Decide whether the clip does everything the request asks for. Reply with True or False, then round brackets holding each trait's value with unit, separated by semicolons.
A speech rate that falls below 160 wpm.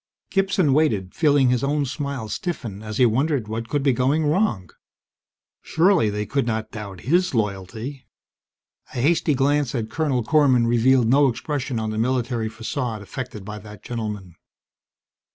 True (150 wpm)